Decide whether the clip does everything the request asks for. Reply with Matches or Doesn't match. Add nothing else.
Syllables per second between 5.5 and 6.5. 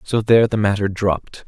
Matches